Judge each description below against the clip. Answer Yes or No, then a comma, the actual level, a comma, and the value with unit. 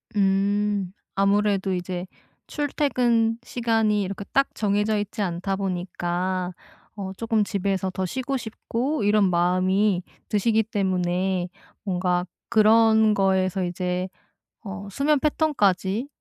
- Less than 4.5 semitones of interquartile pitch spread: Yes, average, 2.9 semitones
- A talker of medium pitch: No, high, 200 Hz